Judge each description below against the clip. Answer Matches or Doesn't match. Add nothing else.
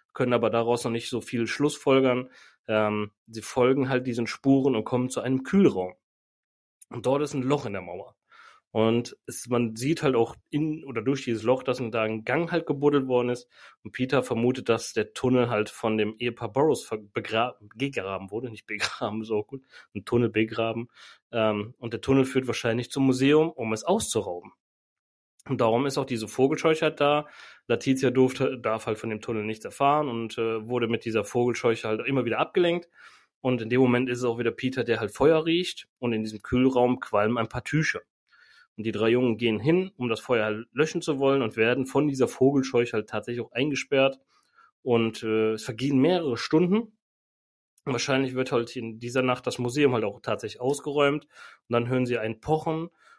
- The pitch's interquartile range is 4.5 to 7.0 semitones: Doesn't match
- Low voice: Matches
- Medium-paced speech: Doesn't match